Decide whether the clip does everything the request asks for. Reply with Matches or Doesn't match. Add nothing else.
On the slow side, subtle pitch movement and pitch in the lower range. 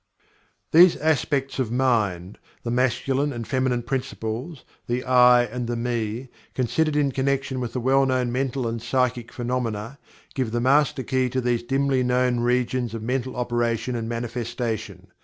Doesn't match